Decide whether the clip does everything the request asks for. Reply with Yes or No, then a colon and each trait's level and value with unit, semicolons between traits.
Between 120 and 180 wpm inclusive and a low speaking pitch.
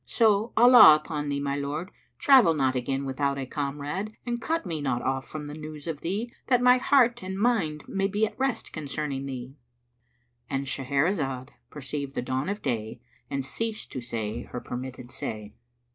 No: average, 175 wpm; medium, 145 Hz